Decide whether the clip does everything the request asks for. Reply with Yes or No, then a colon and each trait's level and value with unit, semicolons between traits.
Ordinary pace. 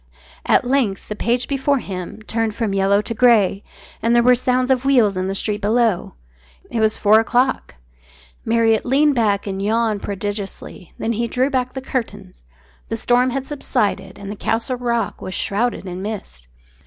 Yes: average, 175 wpm